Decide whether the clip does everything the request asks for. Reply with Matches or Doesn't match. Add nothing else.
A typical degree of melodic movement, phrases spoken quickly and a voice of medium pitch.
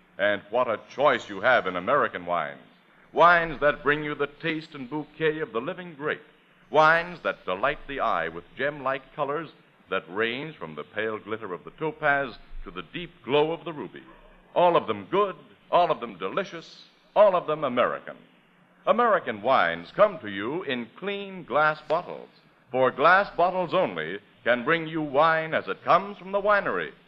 Doesn't match